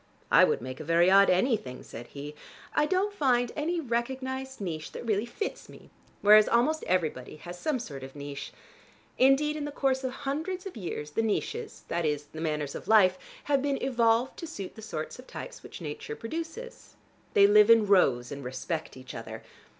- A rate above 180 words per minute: Yes, average, 190 wpm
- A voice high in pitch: Yes, high, 215 Hz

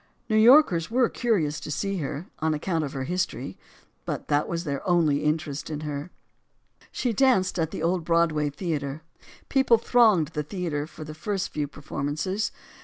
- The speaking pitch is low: No, medium, 160 Hz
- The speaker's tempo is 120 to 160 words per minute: No, average, 170 wpm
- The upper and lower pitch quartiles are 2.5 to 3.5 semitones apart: No, average, 4.3 semitones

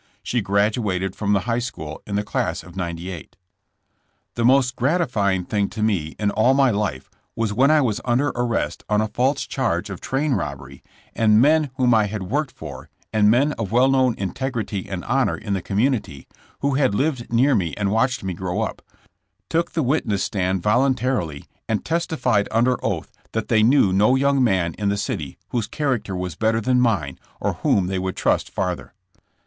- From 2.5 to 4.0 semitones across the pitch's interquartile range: No, average, 4.9 semitones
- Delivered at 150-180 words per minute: No, average, 190 wpm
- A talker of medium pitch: No, low, 110 Hz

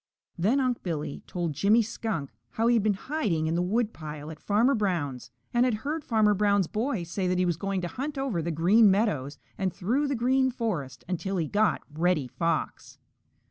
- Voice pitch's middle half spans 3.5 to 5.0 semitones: No, wide, 5.6 semitones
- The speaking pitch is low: No, high, 195 Hz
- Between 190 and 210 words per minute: Yes, average, 195 wpm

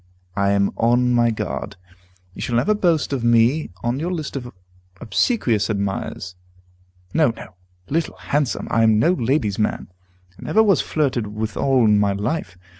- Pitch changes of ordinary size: No, wide, 5.9 semitones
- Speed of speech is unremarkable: Yes, average, 160 wpm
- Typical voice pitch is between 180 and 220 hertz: No, low, 120 Hz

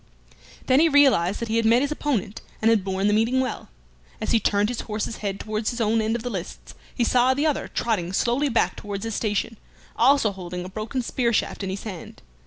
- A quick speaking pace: Yes, fast, 225 wpm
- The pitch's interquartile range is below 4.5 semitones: Yes, average, 3.5 semitones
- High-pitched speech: Yes, high, 225 Hz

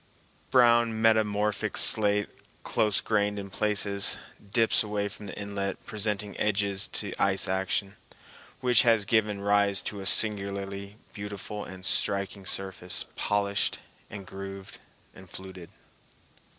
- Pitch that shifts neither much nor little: No, narrow, 1.3 semitones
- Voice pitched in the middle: No, low, 100 Hz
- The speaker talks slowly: Yes, slow, 120 wpm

